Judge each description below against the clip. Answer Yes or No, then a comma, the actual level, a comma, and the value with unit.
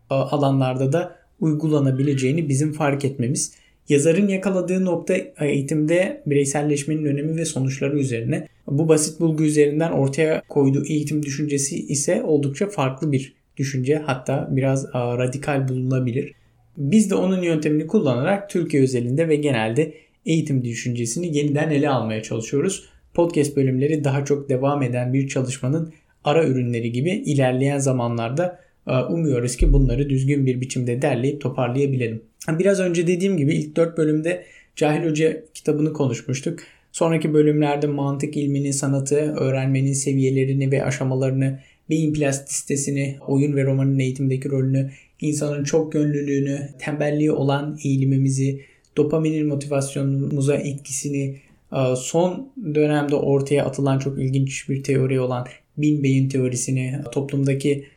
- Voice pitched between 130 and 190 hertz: Yes, medium, 140 Hz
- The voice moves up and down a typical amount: No, narrow, 2.2 semitones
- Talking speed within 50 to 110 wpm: No, average, 120 wpm